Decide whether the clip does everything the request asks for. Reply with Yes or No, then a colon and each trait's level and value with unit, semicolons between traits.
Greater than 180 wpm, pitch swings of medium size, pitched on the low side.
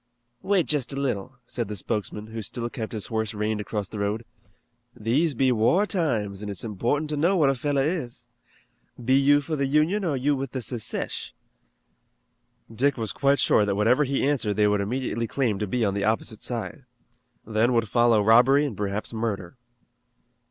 Yes: average, 190 wpm; average, 4.7 semitones; low, 120 Hz